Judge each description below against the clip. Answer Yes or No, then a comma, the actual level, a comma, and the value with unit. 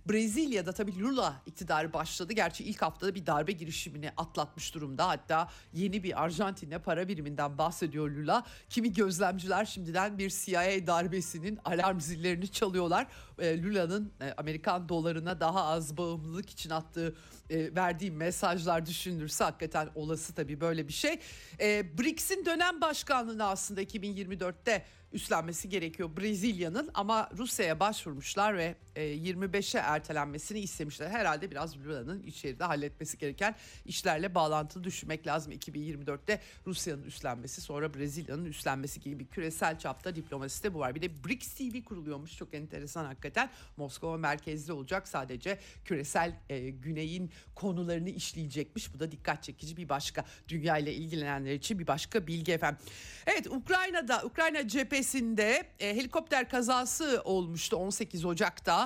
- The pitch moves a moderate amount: Yes, average, 4.5 semitones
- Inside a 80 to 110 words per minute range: No, average, 125 wpm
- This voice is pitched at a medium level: Yes, medium, 175 Hz